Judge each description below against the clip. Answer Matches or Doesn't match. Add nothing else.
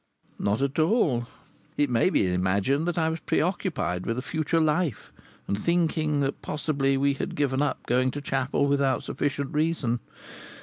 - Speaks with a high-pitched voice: Doesn't match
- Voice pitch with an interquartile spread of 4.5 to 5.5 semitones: Doesn't match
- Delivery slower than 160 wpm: Doesn't match